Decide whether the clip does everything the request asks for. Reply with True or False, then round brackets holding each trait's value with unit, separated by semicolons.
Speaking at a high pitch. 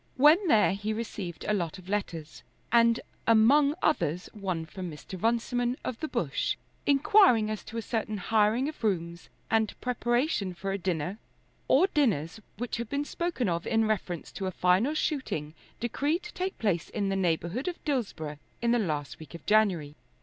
True (215 Hz)